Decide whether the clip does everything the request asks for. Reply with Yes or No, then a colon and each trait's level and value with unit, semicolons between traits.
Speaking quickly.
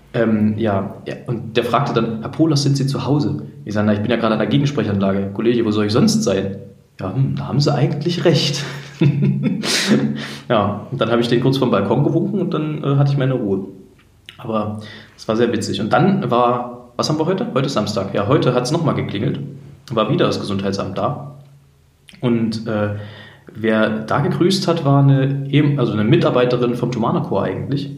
Yes: fast, 200 wpm